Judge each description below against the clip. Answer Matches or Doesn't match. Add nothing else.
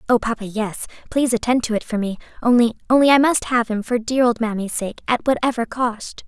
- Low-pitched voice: Doesn't match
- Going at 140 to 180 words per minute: Doesn't match